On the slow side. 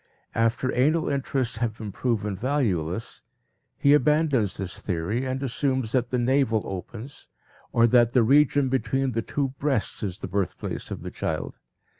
No: average, 155 wpm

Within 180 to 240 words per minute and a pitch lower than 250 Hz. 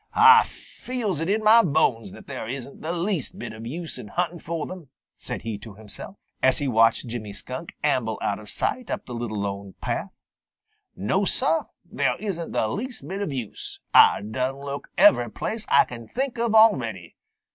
Yes: average, 190 wpm; medium, 140 Hz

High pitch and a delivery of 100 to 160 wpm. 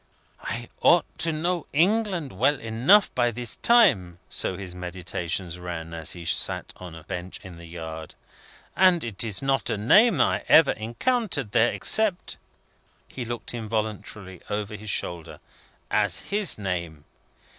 No: low, 110 Hz; average, 150 wpm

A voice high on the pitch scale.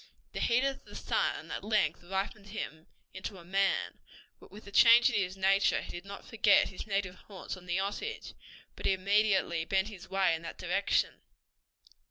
Yes: high, 195 Hz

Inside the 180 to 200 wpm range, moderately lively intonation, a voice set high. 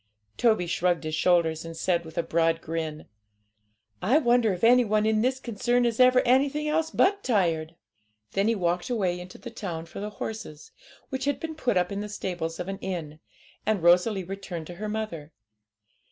No: average, 190 wpm; wide, 5.9 semitones; high, 195 Hz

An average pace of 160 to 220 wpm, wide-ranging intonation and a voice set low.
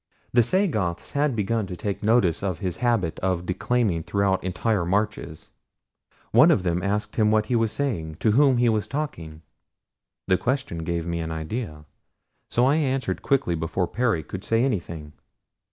Yes: average, 170 wpm; wide, 5.9 semitones; low, 100 Hz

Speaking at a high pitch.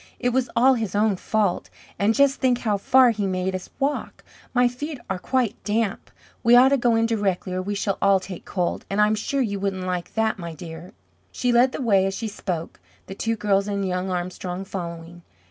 Yes: high, 205 Hz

